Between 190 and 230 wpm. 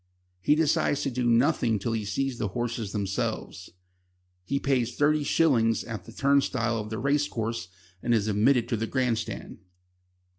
No: average, 165 wpm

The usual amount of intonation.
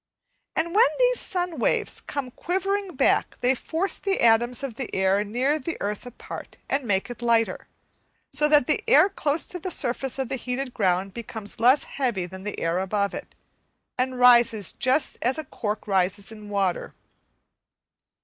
No: wide, 6.2 semitones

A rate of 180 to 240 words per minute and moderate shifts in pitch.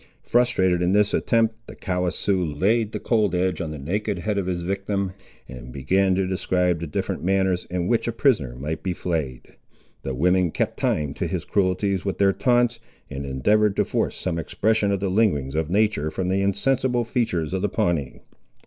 Yes: average, 195 wpm; average, 3.8 semitones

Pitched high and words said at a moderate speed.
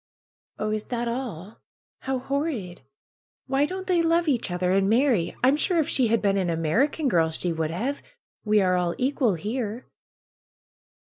Yes: high, 230 Hz; average, 165 wpm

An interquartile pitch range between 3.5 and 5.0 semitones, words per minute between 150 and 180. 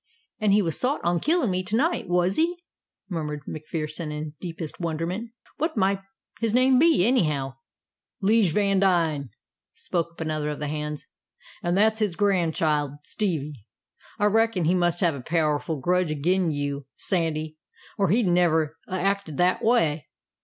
Yes: average, 4.6 semitones; average, 155 wpm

